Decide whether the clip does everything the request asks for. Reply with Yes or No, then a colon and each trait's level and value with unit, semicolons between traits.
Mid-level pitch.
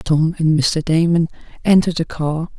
Yes: medium, 160 Hz